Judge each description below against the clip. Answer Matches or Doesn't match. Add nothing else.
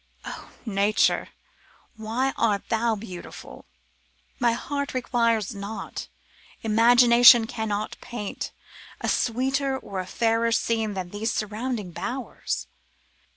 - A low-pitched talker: Doesn't match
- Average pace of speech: Doesn't match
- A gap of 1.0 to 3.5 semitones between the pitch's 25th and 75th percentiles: Matches